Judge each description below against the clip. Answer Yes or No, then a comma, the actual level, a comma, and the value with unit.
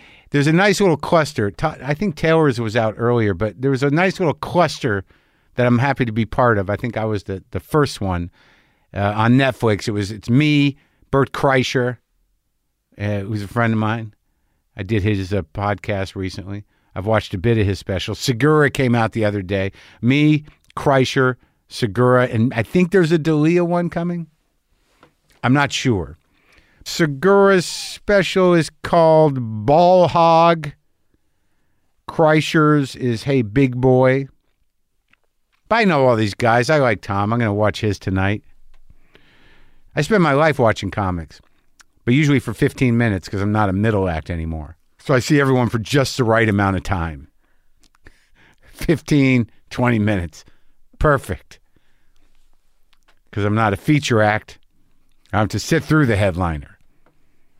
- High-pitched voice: No, low, 120 Hz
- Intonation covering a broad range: Yes, wide, 6.2 semitones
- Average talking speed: Yes, average, 160 wpm